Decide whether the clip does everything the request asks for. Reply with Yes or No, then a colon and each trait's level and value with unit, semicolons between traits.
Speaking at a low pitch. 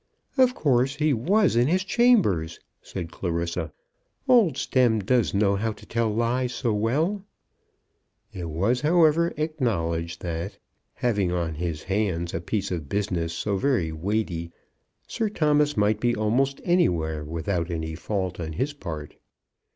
Yes: low, 105 Hz